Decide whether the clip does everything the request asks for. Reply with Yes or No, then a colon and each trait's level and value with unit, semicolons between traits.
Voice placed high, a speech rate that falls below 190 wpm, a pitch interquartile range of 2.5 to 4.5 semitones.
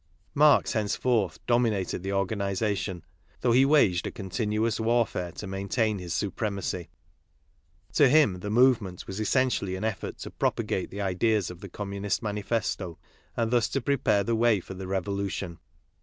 No: low, 105 Hz; average, 155 wpm; average, 3.4 semitones